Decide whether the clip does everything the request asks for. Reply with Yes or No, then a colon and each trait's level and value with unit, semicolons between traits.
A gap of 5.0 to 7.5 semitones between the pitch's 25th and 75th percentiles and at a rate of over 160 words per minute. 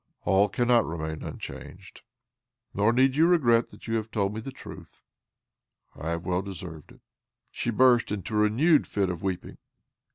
No: average, 4.6 semitones; average, 170 wpm